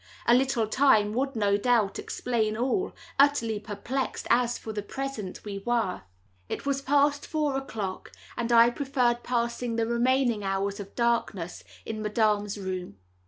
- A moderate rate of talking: Yes, average, 145 wpm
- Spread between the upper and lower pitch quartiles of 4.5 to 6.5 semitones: No, average, 3.9 semitones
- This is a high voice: Yes, high, 235 Hz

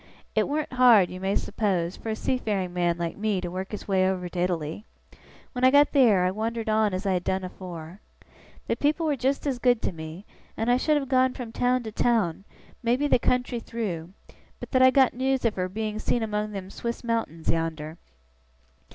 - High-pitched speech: Yes, high, 215 Hz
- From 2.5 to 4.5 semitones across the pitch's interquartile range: No, average, 5.3 semitones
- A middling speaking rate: No, fast, 210 wpm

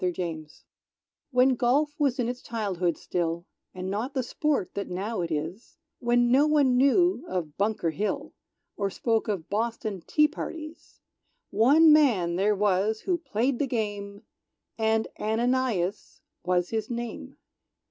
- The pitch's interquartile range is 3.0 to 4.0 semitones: No, wide, 5.5 semitones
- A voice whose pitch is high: Yes, high, 220 Hz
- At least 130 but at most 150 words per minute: Yes, average, 140 wpm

